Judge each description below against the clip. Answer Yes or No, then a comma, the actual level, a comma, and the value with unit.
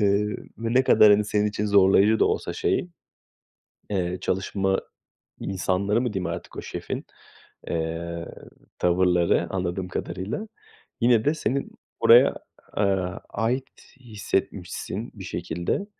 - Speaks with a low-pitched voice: Yes, low, 100 Hz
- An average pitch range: Yes, average, 3.1 semitones